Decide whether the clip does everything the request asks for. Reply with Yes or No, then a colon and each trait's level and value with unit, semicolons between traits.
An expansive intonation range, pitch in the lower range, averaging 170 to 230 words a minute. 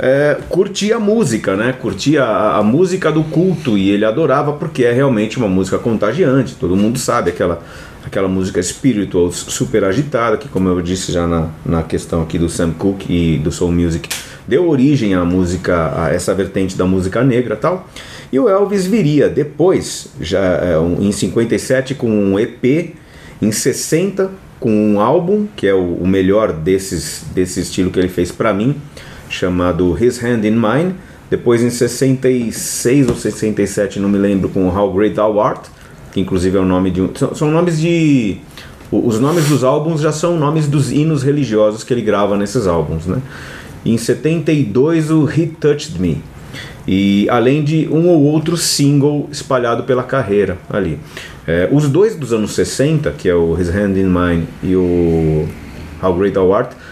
Yes: wide, 7.9 semitones; low, 110 Hz; average, 180 wpm